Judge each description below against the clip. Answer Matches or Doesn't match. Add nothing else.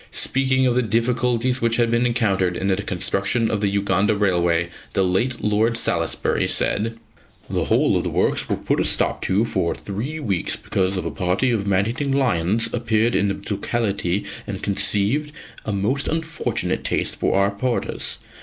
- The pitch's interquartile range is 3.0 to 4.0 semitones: Matches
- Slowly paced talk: Doesn't match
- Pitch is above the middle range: Doesn't match